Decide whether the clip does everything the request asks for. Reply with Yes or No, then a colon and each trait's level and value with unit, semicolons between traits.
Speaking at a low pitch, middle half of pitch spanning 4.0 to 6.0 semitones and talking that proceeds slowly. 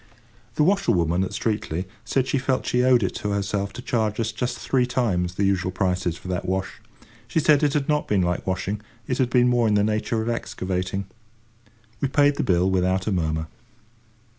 No: low, 105 Hz; average, 5.1 semitones; average, 200 wpm